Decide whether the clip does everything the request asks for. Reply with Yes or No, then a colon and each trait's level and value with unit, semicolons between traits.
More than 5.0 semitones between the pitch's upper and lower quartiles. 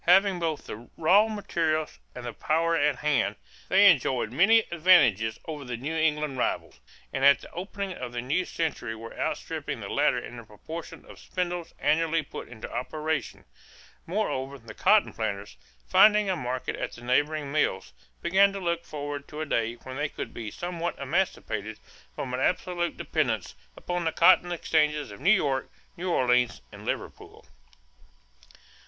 Yes: wide, 5.6 semitones